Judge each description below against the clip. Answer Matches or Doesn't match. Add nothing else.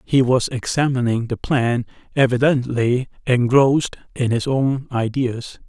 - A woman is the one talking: Doesn't match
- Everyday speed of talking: Doesn't match